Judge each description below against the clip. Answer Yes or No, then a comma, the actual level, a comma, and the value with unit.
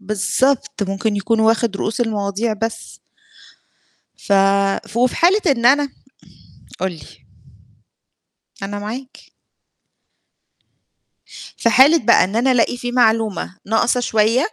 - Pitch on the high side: Yes, high, 225 Hz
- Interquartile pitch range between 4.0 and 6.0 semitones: No, average, 3.2 semitones